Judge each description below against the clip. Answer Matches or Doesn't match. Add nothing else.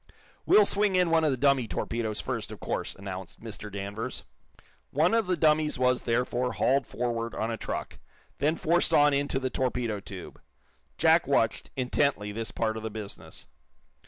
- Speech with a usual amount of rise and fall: Matches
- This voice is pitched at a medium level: Doesn't match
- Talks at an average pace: Matches